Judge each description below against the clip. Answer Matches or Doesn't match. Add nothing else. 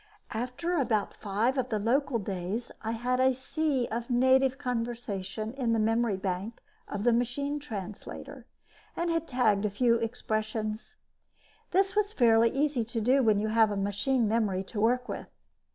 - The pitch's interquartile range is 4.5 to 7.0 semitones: Doesn't match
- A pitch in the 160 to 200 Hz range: Doesn't match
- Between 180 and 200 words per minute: Doesn't match